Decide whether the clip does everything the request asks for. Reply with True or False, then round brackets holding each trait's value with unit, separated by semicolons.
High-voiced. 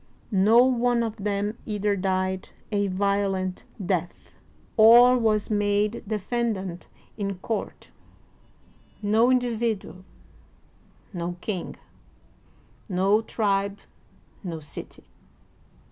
True (205 Hz)